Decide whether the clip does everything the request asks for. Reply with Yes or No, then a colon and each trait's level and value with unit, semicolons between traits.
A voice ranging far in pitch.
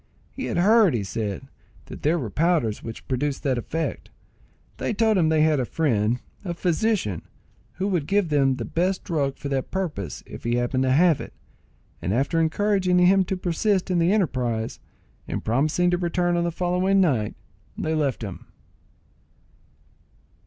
Yes: wide, 5.9 semitones